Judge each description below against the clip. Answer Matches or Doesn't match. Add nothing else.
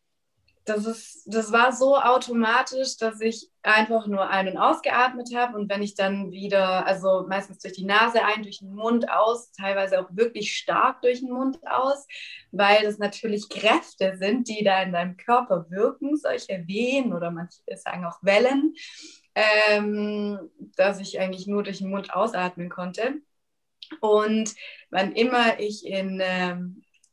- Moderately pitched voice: Doesn't match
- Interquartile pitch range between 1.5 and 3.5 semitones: Doesn't match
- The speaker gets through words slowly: Doesn't match